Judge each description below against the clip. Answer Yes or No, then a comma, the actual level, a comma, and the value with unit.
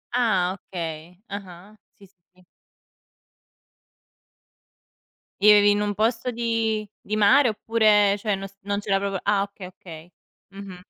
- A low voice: No, high, 200 Hz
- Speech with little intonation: Yes, narrow, 2.2 semitones